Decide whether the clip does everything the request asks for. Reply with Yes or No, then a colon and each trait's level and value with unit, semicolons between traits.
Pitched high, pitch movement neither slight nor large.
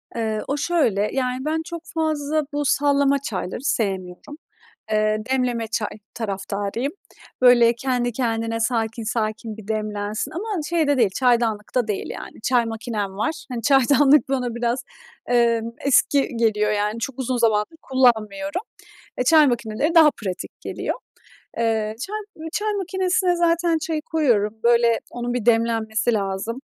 Yes: high, 240 Hz; average, 4.7 semitones